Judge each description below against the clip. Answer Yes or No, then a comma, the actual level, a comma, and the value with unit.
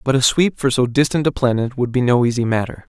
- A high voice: No, low, 125 Hz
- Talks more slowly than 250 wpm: No, fast, 265 wpm